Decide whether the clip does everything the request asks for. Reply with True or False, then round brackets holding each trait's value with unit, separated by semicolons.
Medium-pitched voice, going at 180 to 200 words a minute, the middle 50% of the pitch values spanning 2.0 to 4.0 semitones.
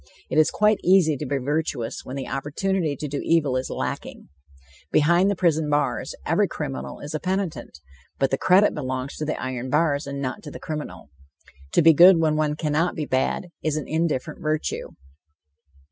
True (150 Hz; 185 wpm; 3.3 semitones)